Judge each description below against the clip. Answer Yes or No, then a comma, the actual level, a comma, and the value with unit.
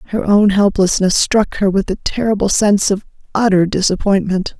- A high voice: Yes, high, 200 Hz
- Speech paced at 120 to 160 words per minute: Yes, average, 155 wpm